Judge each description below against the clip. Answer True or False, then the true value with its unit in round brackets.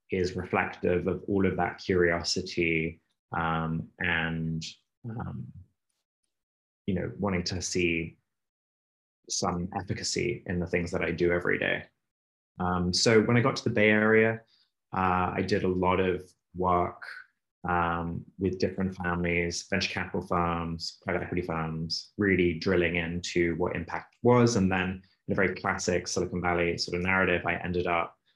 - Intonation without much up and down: True (1.9 semitones)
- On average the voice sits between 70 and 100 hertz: True (90 Hz)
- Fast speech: False (150 wpm)